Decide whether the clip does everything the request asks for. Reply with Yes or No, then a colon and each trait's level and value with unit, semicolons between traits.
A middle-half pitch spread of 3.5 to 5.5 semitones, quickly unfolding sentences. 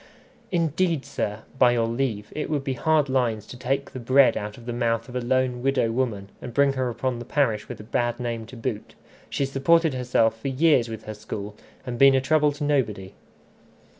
No: average, 3.1 semitones; fast, 210 wpm